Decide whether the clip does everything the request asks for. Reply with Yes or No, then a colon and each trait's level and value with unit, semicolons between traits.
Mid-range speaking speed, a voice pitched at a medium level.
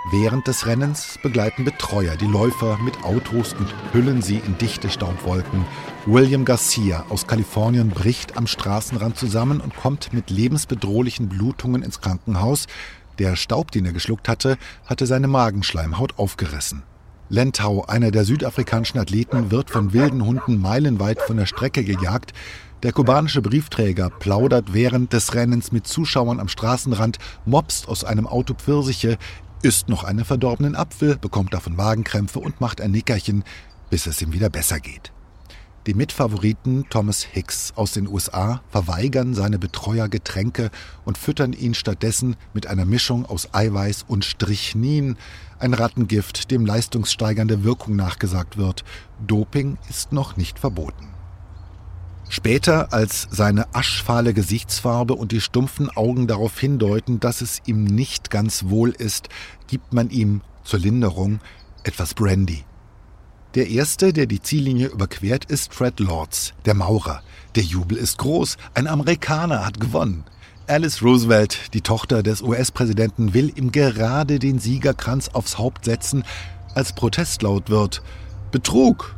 No: average, 140 wpm; low, 110 Hz